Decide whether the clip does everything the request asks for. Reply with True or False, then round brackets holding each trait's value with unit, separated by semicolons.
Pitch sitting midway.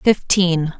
True (180 Hz)